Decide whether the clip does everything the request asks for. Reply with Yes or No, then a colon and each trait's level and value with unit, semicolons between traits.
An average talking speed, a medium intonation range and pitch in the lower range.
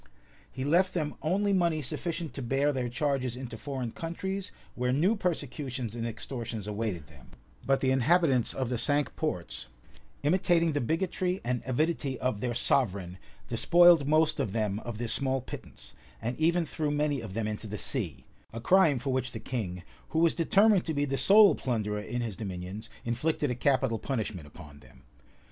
No: average, 180 wpm; wide, 5.8 semitones; low, 130 Hz